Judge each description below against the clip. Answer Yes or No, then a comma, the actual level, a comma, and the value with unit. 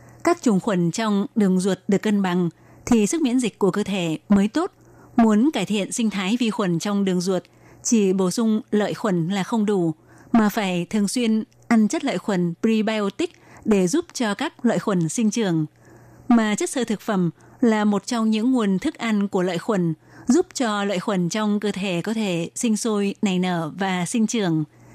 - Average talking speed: Yes, average, 200 wpm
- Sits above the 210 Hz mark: No, high, 205 Hz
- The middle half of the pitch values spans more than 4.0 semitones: No, average, 3.6 semitones